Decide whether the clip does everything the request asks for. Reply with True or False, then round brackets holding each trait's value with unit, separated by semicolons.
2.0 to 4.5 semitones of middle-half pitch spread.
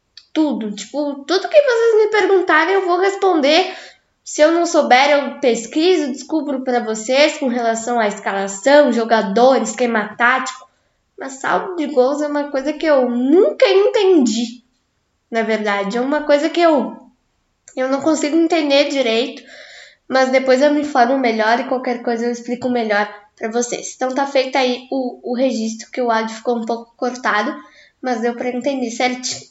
True (3.8 semitones)